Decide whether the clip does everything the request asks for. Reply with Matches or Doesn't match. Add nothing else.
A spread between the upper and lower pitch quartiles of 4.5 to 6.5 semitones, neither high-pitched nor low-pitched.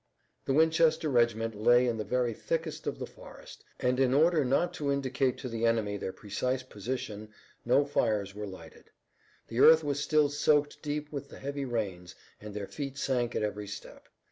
Doesn't match